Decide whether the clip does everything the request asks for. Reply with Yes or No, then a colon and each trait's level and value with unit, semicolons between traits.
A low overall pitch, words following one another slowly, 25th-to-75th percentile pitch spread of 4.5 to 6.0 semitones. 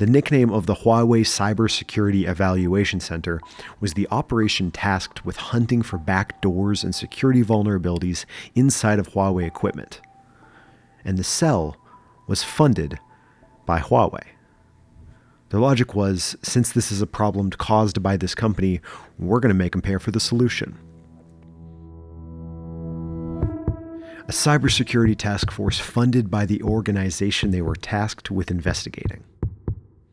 No: low, 100 Hz; slow, 125 wpm; average, 3.8 semitones